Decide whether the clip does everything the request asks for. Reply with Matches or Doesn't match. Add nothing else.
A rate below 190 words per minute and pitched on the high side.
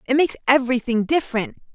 Matches